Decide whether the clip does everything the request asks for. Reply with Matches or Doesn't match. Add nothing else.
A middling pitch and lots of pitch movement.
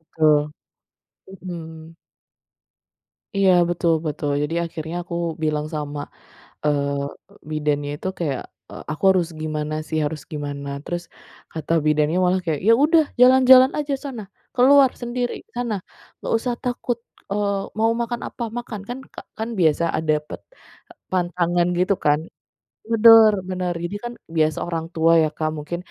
Matches